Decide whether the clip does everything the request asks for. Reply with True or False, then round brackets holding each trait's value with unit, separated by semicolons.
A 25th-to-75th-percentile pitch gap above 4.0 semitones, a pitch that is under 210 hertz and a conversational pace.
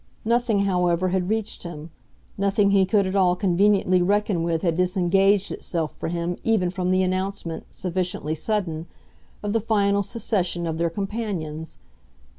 False (2.7 semitones; 185 Hz; 150 wpm)